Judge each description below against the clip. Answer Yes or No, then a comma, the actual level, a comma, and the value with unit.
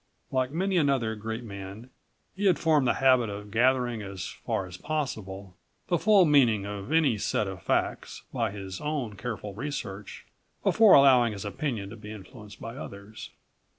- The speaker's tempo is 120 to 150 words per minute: No, average, 165 wpm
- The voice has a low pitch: Yes, low, 115 Hz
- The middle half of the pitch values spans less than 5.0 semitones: No, wide, 5.4 semitones